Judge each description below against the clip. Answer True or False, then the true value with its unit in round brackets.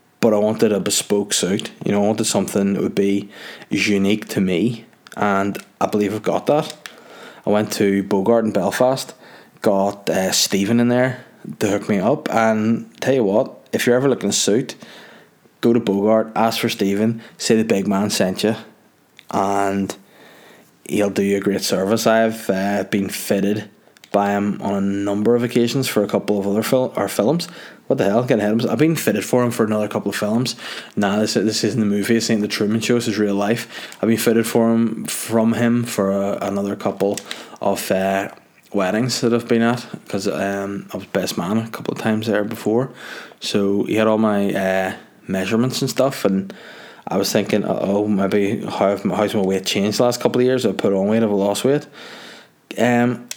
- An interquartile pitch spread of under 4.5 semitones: True (2.7 semitones)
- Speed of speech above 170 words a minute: True (205 wpm)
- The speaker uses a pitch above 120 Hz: False (105 Hz)